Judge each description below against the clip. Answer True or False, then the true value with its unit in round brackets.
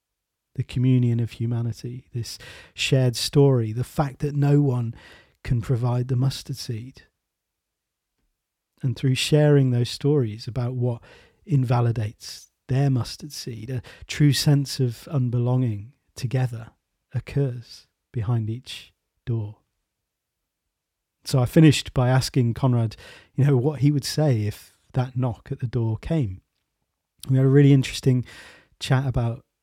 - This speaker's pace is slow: True (130 wpm)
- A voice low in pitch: True (125 Hz)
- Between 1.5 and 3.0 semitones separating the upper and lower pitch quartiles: True (2.7 semitones)